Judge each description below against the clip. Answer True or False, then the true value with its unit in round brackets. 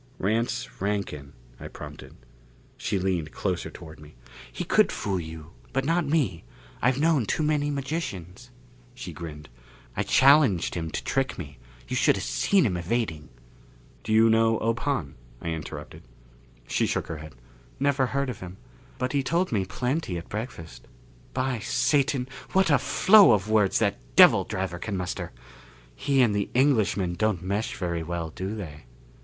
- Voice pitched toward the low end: True (105 Hz)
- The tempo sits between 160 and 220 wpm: True (165 wpm)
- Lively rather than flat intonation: True (7.5 semitones)